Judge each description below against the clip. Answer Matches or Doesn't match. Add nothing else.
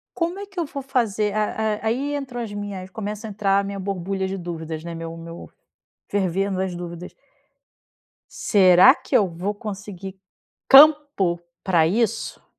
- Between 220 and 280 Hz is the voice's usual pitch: Doesn't match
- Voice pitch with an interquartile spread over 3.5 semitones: Matches